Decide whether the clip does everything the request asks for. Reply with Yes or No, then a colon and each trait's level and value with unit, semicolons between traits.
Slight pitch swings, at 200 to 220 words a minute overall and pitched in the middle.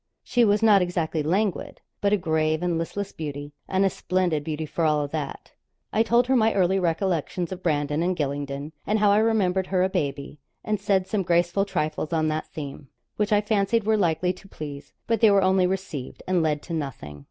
No: average, 4.4 semitones; fast, 205 wpm; medium, 180 Hz